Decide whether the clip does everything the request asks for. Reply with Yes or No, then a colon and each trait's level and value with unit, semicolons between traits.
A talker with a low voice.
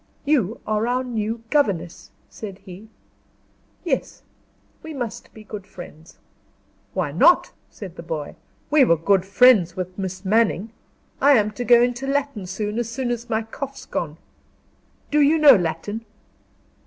No: high, 220 Hz